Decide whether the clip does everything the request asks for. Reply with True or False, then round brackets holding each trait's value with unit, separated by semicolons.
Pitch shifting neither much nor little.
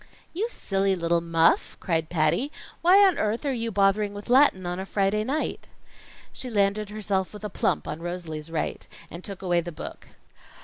True (3.8 semitones)